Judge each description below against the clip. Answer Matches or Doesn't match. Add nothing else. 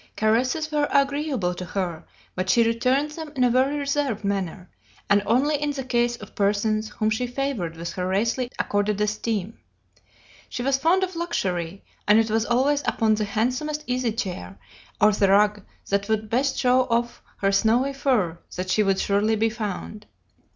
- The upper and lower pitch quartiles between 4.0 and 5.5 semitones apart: Matches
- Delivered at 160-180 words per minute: Matches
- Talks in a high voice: Matches